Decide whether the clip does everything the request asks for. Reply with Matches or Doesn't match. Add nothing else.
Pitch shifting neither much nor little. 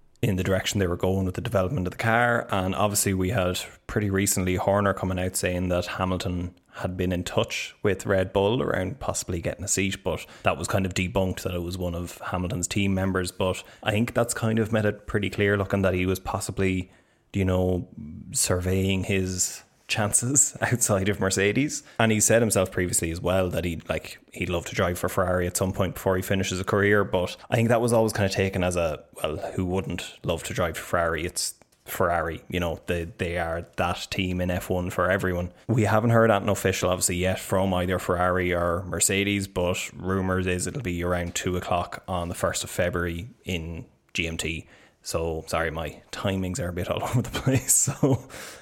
Doesn't match